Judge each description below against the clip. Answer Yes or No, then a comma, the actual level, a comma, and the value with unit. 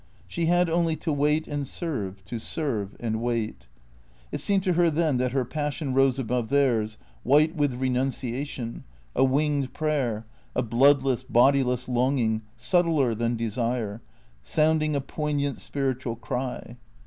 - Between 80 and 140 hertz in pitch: Yes, low, 135 Hz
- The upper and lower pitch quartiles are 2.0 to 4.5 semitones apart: Yes, average, 4.0 semitones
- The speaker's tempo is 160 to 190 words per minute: No, average, 140 wpm